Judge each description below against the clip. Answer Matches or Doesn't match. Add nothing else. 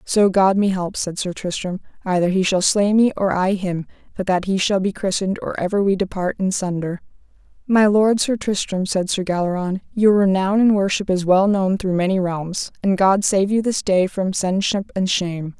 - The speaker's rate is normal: Doesn't match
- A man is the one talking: Doesn't match